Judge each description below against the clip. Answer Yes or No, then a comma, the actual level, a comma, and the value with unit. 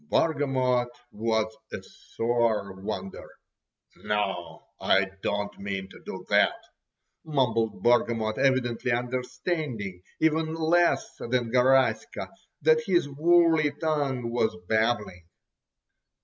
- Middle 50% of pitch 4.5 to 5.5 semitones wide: Yes, average, 4.9 semitones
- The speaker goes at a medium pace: No, slow, 95 wpm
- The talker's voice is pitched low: Yes, low, 120 Hz